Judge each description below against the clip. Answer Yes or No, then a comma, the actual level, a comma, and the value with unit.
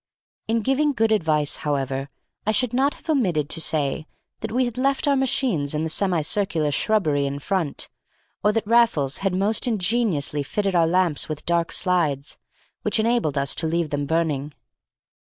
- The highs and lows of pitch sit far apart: Yes, wide, 7.0 semitones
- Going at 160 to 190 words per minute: Yes, average, 170 wpm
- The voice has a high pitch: No, medium, 175 Hz